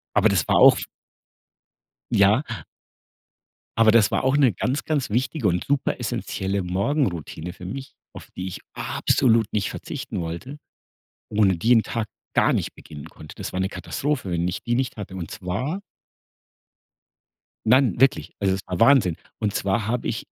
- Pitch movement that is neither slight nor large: No, wide, 5.7 semitones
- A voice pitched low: Yes, low, 105 Hz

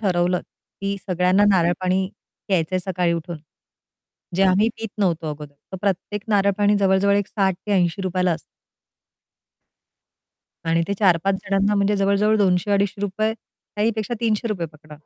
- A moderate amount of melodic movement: No, narrow, 2.2 semitones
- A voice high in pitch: Yes, high, 195 Hz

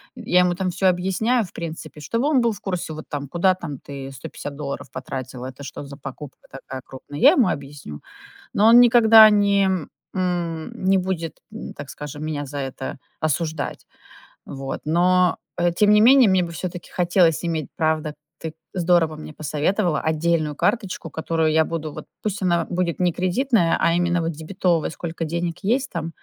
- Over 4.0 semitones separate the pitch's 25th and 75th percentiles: No, average, 3.7 semitones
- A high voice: No, medium, 170 Hz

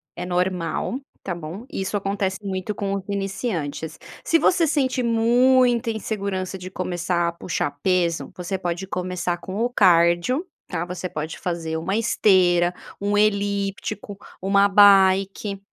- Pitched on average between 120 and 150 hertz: No, high, 190 Hz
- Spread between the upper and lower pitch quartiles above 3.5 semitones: No, narrow, 2.6 semitones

